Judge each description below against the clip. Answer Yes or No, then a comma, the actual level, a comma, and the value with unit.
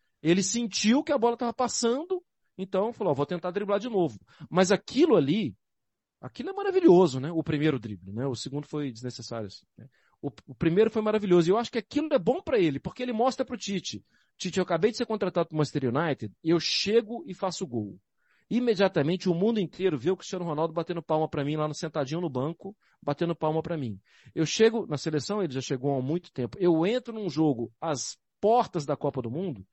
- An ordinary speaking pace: No, fast, 215 wpm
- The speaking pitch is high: No, medium, 175 Hz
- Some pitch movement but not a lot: No, wide, 6.7 semitones